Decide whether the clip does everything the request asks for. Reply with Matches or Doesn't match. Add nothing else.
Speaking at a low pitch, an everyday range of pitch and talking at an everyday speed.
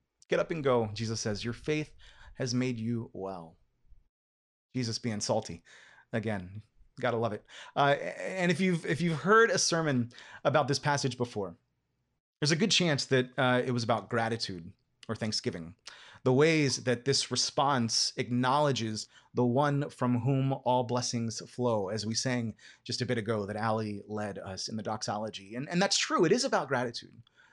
Matches